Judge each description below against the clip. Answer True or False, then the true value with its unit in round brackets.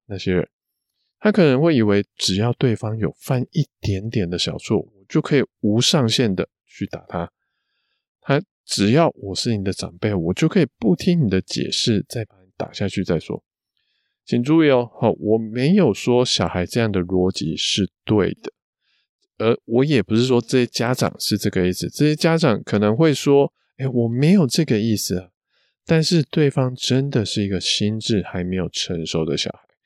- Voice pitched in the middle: False (115 Hz)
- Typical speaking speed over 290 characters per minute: False (255 characters per minute)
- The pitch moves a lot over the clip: True (5.8 semitones)